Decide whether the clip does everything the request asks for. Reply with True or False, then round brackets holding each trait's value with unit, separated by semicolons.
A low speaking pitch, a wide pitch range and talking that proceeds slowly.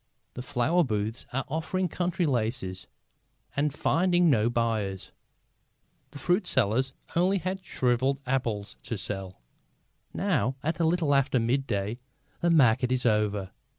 True (130 Hz; 6.4 semitones; 130 wpm)